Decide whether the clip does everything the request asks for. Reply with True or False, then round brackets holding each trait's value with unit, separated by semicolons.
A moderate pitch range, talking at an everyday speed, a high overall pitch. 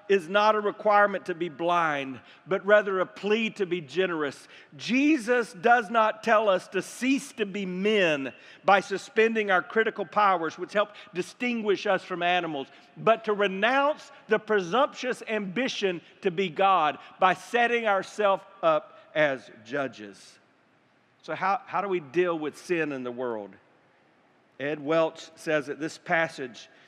True (4.4 semitones; 150 wpm; 195 Hz)